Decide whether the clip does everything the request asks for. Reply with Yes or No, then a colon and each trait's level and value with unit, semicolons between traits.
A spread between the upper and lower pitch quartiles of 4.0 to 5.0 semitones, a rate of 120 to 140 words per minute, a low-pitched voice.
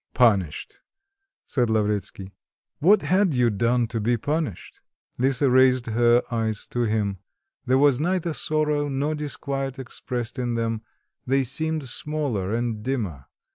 Yes: average, 4.4 semitones; slow, 135 wpm; low, 125 Hz